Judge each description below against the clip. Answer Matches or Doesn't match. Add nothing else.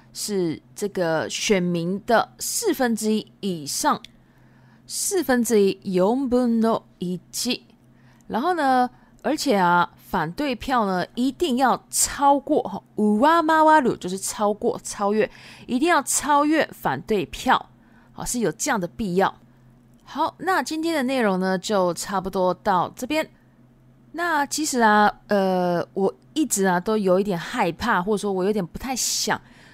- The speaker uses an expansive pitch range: Matches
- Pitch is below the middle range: Doesn't match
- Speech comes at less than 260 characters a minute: Matches